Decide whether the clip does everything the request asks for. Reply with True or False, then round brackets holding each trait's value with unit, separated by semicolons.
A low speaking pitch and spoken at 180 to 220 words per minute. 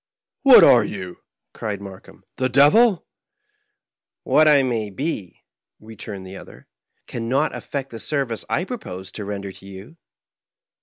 False (115 Hz; 170 wpm)